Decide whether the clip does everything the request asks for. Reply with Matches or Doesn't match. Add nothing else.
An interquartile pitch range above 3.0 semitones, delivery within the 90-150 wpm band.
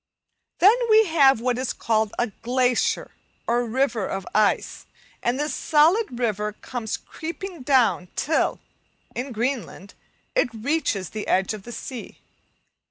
Matches